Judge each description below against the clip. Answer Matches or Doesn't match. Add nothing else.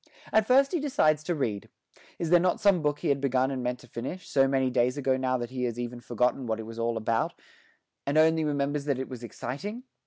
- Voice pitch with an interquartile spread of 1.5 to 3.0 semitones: Doesn't match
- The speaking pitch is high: Doesn't match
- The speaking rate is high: Matches